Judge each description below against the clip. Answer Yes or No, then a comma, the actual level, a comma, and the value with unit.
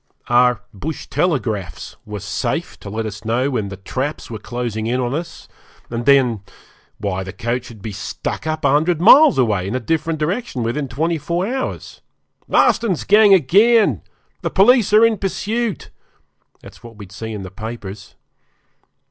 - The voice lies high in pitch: No, low, 125 Hz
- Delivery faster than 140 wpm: Yes, average, 165 wpm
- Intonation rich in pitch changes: Yes, wide, 7.9 semitones